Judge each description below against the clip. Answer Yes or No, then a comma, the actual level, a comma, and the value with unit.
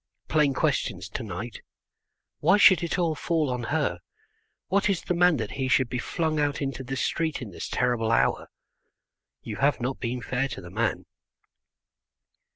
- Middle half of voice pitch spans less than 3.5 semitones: No, average, 5.0 semitones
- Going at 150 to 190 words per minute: Yes, average, 170 wpm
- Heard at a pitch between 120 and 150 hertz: Yes, low, 135 Hz